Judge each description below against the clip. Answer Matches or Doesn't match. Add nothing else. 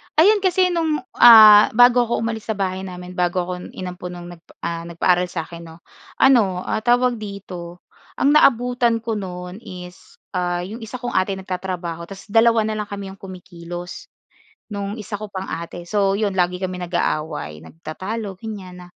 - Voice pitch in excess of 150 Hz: Matches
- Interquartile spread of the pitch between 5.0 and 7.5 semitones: Doesn't match